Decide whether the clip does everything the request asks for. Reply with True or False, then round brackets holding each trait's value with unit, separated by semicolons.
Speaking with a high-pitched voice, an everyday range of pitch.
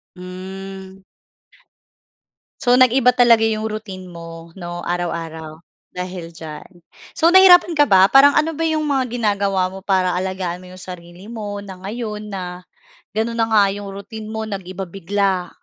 True (195 Hz; 3.6 semitones)